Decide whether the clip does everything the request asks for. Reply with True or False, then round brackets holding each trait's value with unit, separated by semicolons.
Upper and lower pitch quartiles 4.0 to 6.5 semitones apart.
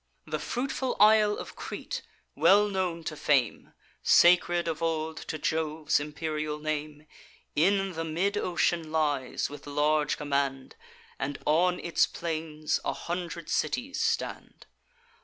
False (2.9 semitones)